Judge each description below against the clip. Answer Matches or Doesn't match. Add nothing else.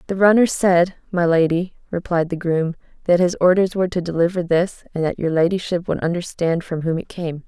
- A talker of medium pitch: Matches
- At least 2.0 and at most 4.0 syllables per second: Doesn't match